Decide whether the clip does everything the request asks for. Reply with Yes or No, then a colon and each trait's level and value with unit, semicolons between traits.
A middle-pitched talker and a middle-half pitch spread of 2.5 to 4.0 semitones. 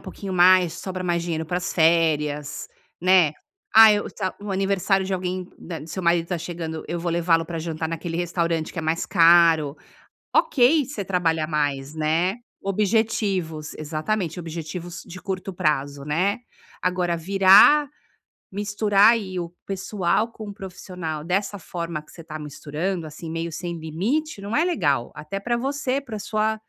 Yes: medium, 175 Hz; average, 3.5 semitones